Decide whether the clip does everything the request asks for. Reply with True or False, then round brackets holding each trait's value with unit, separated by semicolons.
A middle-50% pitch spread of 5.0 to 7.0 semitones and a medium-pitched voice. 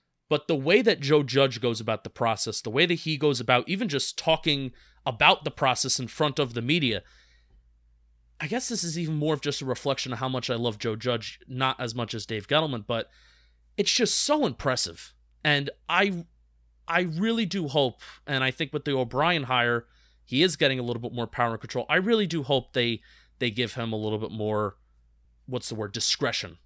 False (5.6 semitones; 125 Hz)